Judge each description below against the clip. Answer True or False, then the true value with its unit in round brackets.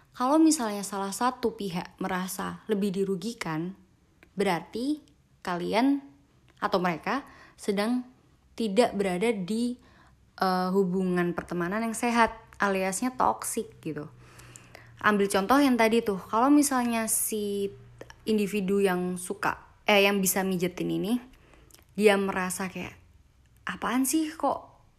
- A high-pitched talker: True (200 Hz)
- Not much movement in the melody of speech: False (4.0 semitones)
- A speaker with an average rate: True (110 wpm)